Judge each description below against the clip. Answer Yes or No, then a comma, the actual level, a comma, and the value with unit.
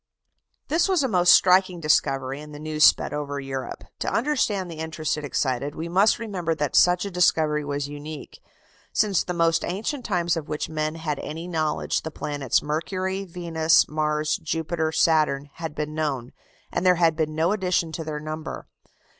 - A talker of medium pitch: Yes, medium, 160 Hz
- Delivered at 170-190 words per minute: Yes, average, 180 wpm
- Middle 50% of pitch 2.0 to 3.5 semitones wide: Yes, average, 2.8 semitones